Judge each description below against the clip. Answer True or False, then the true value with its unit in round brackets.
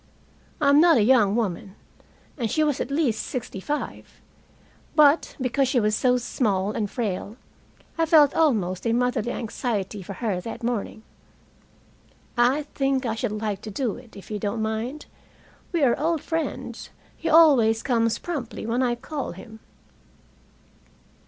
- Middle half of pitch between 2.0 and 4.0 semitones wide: False (4.5 semitones)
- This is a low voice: False (240 Hz)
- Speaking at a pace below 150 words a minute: False (155 wpm)